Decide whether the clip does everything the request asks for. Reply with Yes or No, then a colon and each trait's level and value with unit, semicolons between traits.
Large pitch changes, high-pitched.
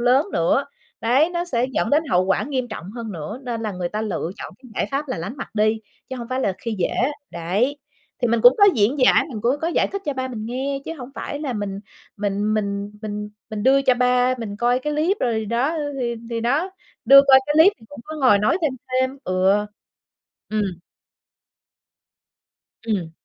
No: average, 4.6 semitones; high, 240 Hz